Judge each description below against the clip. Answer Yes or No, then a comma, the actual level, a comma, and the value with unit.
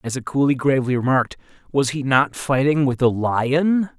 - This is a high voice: No, low, 135 Hz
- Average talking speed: Yes, average, 180 wpm